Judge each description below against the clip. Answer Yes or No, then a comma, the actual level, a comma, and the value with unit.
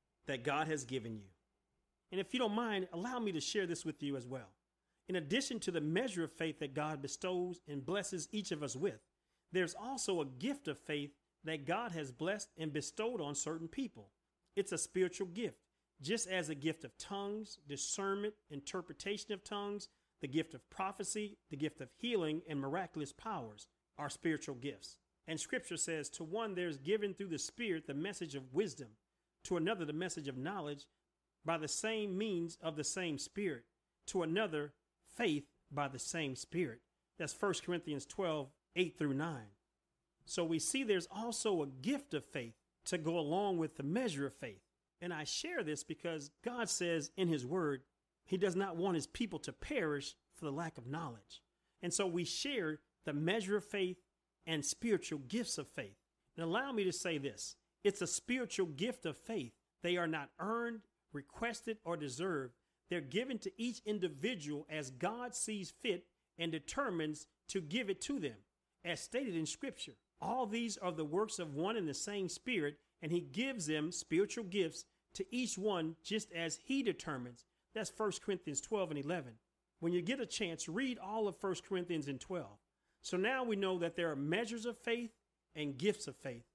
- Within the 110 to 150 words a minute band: No, average, 185 wpm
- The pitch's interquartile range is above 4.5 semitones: Yes, average, 5.1 semitones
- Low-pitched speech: No, medium, 175 Hz